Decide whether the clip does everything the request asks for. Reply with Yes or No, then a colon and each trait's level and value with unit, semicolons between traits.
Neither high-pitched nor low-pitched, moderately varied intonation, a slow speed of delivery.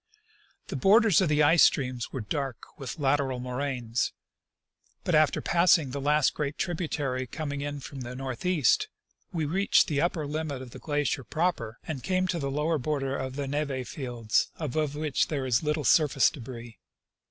No: medium, 145 Hz; average, 3.1 semitones; average, 175 wpm